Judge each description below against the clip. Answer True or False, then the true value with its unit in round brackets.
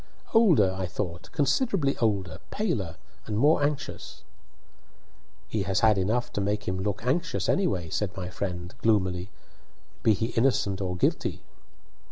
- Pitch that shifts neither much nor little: False (6.4 semitones)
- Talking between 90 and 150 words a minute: True (140 wpm)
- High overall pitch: False (105 Hz)